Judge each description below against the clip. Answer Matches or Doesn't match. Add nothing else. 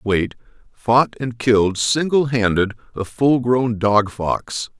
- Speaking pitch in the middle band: Doesn't match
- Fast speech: Doesn't match